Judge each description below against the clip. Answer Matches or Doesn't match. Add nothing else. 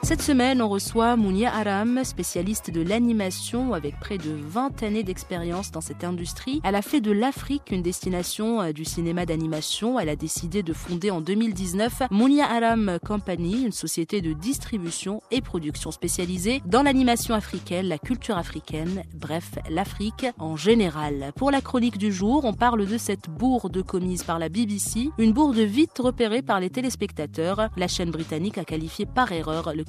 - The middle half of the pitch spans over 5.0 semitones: Matches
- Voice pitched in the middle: Doesn't match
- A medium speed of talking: Matches